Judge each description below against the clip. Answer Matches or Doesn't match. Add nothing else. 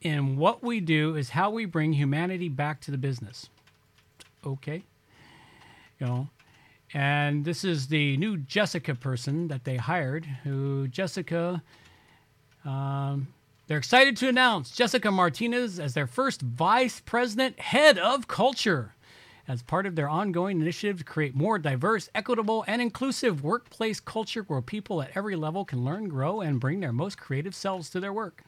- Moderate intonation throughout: Doesn't match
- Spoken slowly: Doesn't match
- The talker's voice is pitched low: Doesn't match